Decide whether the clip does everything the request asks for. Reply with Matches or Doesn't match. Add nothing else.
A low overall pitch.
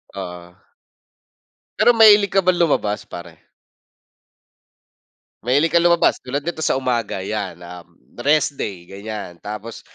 Matches